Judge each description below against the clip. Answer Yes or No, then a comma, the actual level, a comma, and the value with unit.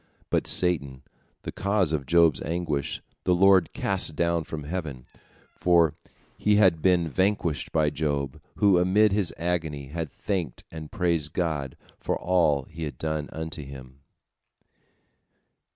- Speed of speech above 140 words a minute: No, slow, 135 wpm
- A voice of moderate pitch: No, very low, 80 Hz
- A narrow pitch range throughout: No, average, 3.4 semitones